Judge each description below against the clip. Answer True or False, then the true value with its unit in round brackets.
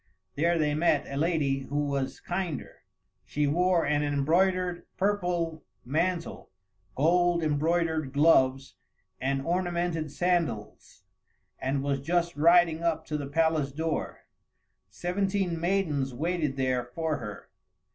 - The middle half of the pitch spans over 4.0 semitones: False (3.7 semitones)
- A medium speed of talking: False (115 wpm)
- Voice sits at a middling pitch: True (160 Hz)